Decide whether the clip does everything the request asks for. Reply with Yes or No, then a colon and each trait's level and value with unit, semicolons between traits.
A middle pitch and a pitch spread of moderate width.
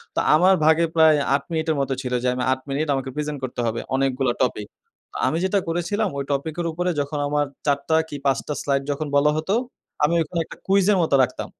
Yes: medium, 150 Hz; average, 3.2 semitones